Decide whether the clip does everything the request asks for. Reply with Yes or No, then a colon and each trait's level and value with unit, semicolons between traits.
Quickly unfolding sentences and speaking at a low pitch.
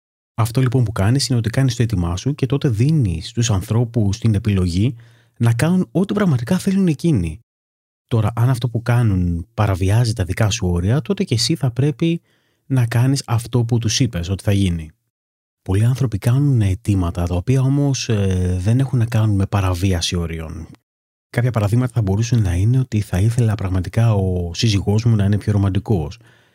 Yes: fast, 180 wpm; low, 115 Hz